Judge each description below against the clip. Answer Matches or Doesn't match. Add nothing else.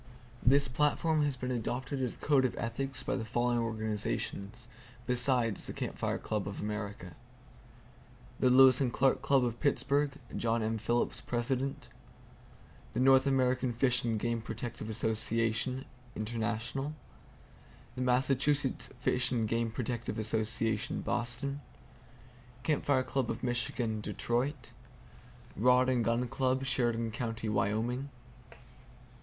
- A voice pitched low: Matches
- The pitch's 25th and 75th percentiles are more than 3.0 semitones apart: Doesn't match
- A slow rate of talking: Matches